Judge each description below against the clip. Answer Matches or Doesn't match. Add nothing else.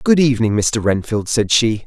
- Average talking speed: Matches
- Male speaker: Matches